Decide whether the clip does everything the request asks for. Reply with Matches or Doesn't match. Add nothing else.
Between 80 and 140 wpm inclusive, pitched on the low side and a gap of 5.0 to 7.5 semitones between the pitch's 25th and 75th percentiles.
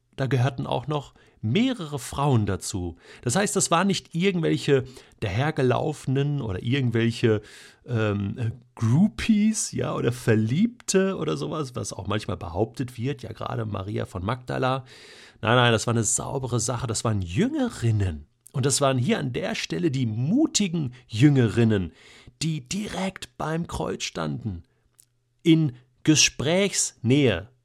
Matches